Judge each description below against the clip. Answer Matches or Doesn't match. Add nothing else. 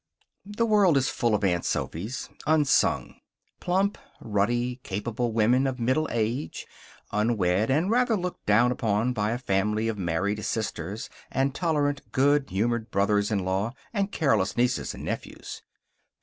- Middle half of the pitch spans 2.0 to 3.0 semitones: Doesn't match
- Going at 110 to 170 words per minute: Matches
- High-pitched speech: Doesn't match